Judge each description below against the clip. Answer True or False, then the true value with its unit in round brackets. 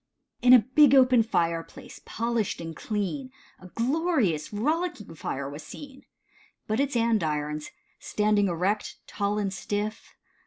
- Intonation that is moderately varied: False (6.1 semitones)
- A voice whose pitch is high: True (215 Hz)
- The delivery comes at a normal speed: False (125 wpm)